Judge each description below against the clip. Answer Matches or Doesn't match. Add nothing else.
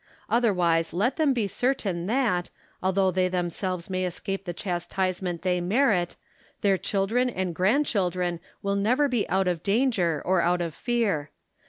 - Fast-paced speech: Doesn't match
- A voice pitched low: Doesn't match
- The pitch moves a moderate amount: Matches